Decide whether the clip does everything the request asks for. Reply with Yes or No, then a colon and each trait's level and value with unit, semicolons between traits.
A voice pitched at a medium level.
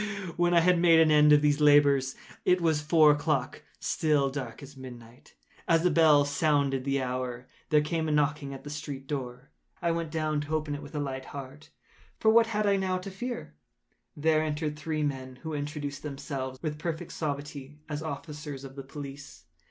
Yes: medium, 150 Hz